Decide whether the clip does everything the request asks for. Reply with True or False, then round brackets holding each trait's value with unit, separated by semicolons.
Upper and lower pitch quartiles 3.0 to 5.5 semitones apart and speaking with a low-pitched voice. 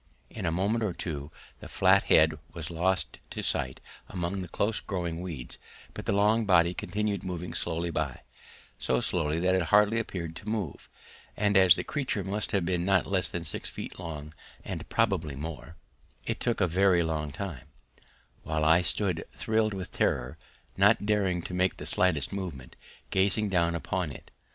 True (3.5 semitones; 90 Hz)